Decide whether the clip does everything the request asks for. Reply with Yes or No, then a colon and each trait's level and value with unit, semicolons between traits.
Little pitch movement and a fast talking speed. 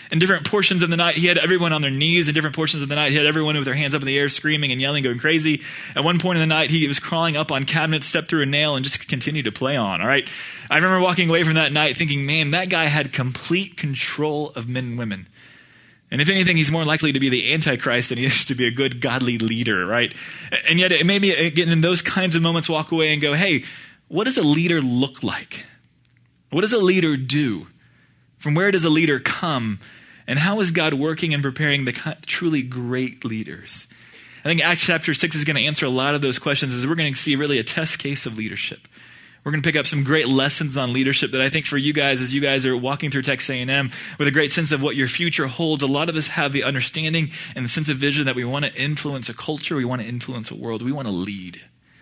No: average, 3.3 semitones; fast, 265 wpm